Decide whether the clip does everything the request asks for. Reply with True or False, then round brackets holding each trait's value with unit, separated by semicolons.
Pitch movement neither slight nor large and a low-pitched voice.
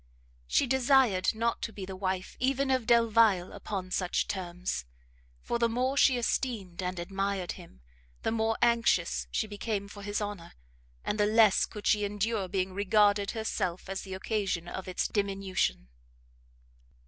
False (3.4 semitones; 205 Hz)